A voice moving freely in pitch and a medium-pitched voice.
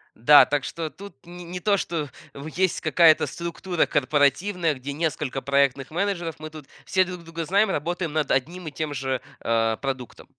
No: average, 4.0 semitones; medium, 155 Hz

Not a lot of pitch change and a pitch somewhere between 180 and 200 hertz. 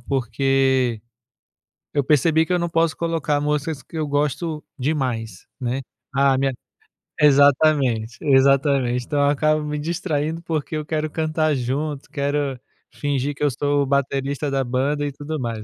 No: narrow, 2.3 semitones; medium, 145 Hz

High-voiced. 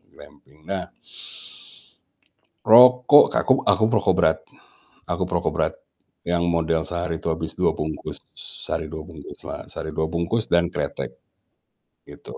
No: very low, 85 Hz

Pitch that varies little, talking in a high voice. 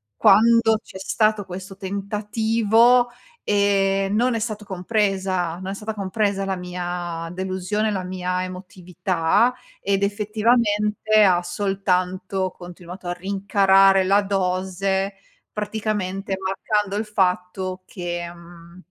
Yes: narrow, 2.3 semitones; high, 195 Hz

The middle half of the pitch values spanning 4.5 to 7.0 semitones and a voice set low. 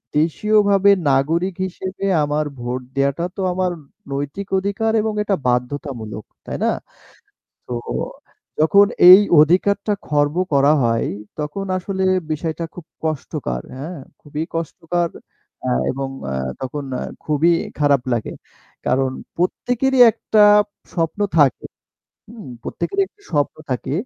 No: wide, 5.6 semitones; medium, 160 Hz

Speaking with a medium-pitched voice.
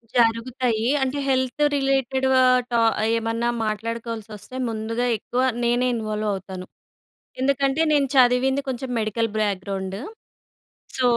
No: high, 235 Hz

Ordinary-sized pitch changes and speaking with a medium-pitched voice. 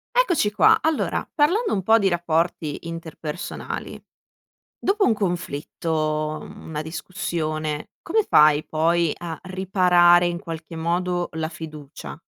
Yes: average, 3.1 semitones; medium, 170 Hz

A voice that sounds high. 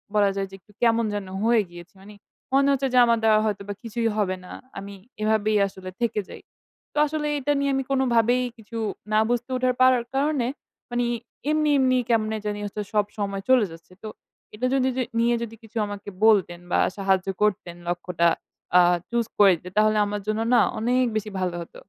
Yes: high, 220 Hz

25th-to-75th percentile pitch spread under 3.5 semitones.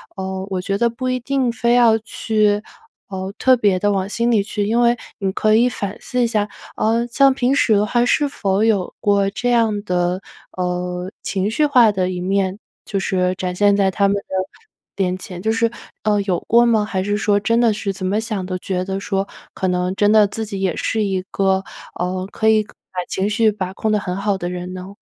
Yes: average, 3.0 semitones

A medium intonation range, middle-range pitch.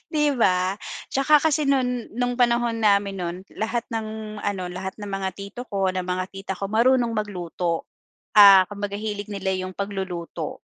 No: average, 3.7 semitones; high, 205 Hz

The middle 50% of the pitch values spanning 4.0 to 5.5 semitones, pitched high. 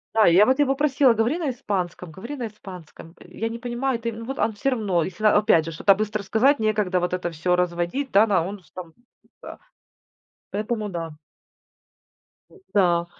Yes: average, 4.9 semitones; high, 210 Hz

